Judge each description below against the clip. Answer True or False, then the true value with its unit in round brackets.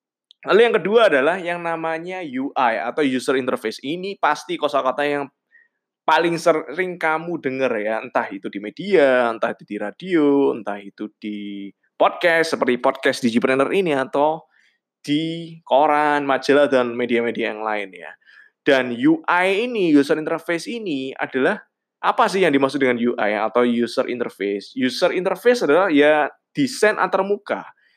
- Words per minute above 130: True (140 wpm)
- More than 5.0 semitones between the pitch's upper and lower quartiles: True (5.6 semitones)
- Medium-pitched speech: True (145 Hz)